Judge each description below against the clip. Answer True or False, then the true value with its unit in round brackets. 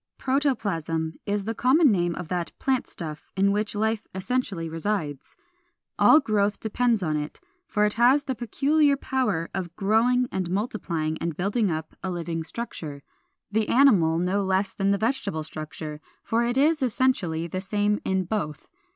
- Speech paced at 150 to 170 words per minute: True (160 wpm)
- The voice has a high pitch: True (200 Hz)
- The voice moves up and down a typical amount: False (6.2 semitones)